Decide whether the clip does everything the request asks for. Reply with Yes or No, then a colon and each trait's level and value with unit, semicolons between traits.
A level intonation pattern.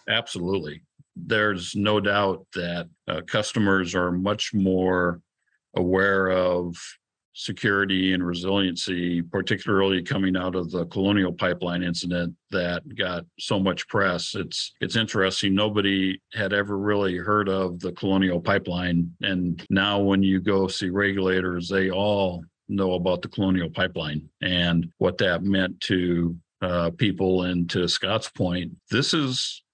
Yes: narrow, 2.0 semitones